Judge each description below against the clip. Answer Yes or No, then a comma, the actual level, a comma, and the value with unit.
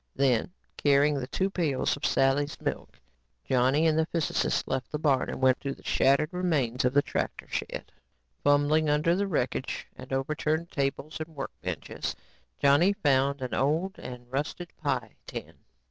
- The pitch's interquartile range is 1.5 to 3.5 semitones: Yes, average, 2.9 semitones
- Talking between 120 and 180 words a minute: Yes, average, 155 wpm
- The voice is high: No, medium, 145 Hz